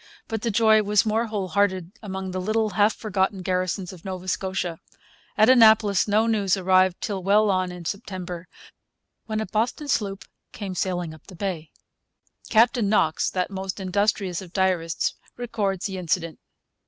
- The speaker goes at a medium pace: Yes, average, 160 wpm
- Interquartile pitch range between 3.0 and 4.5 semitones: No, narrow, 2.6 semitones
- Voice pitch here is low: No, high, 195 Hz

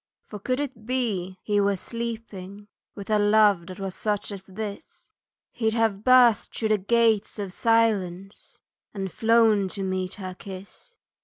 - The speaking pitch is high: Yes, high, 205 Hz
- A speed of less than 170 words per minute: Yes, average, 155 wpm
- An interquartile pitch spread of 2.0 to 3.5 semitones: Yes, average, 2.8 semitones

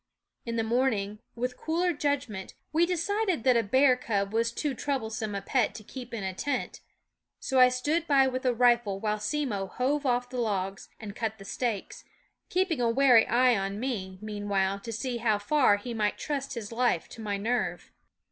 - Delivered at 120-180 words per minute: No, average, 190 wpm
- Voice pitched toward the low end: No, high, 235 Hz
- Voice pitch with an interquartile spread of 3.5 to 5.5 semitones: Yes, average, 4.2 semitones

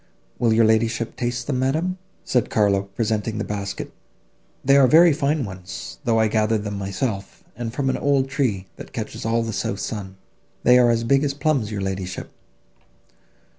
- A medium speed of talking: Yes, average, 175 wpm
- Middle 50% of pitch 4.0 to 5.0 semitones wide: Yes, average, 4.5 semitones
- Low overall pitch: Yes, low, 115 Hz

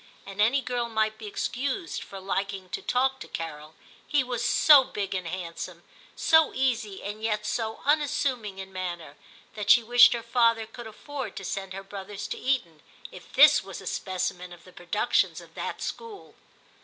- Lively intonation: No, average, 4.5 semitones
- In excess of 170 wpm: Yes, average, 180 wpm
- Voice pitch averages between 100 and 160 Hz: No, high, 215 Hz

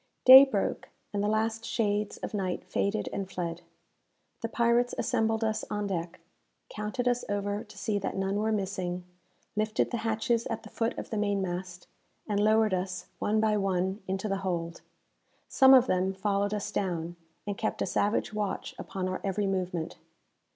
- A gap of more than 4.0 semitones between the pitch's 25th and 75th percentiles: No, average, 2.7 semitones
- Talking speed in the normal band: Yes, average, 170 wpm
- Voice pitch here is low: No, high, 205 Hz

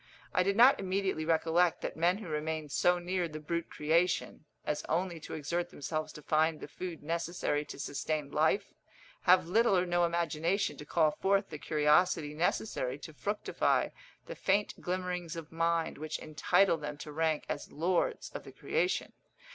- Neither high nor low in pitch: Yes, medium, 165 Hz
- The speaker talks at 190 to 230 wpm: No, average, 170 wpm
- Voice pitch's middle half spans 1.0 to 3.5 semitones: Yes, average, 2.8 semitones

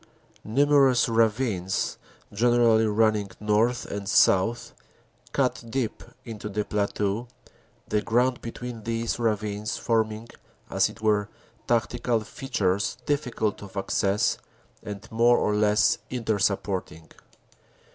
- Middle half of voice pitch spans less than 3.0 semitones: Yes, narrow, 2.5 semitones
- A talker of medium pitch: No, low, 110 Hz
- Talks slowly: Yes, slow, 110 wpm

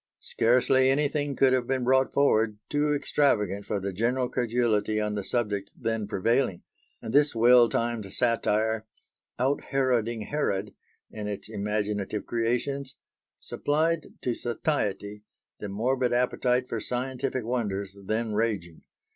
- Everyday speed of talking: No, slow, 130 wpm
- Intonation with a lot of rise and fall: No, average, 3.7 semitones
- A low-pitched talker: Yes, low, 115 Hz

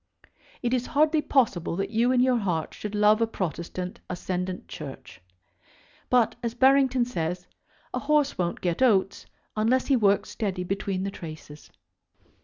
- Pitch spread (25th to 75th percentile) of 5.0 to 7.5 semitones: Yes, wide, 5.6 semitones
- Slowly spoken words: No, average, 150 wpm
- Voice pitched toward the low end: No, high, 210 Hz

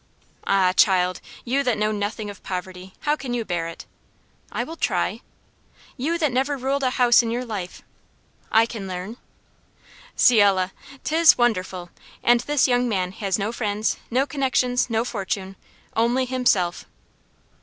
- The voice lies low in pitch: No, high, 225 Hz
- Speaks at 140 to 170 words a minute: Yes, average, 155 wpm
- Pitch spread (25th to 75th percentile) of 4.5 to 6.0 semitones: Yes, average, 4.8 semitones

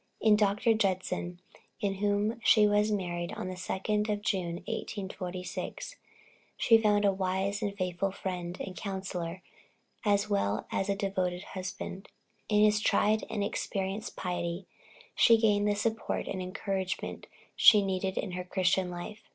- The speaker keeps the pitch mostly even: Yes, narrow, 2.1 semitones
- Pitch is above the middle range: Yes, high, 195 Hz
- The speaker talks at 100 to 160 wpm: Yes, average, 145 wpm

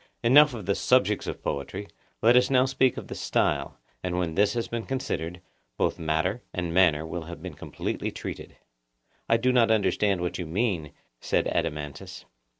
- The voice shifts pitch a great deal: Yes, wide, 5.9 semitones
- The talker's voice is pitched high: No, low, 100 Hz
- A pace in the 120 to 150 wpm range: No, average, 175 wpm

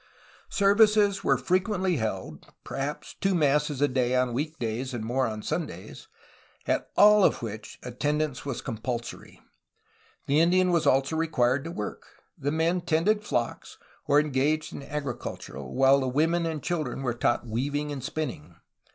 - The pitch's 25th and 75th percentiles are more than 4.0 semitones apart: Yes, average, 4.7 semitones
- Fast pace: No, average, 160 wpm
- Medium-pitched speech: Yes, medium, 145 Hz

